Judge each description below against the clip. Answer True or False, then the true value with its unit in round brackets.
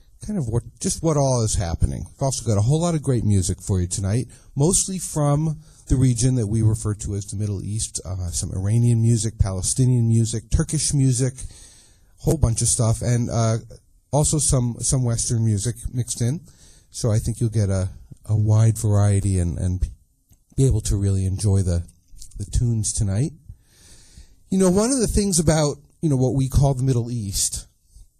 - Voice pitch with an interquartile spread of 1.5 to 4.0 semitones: False (5.0 semitones)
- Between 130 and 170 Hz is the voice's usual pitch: False (115 Hz)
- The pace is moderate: True (190 wpm)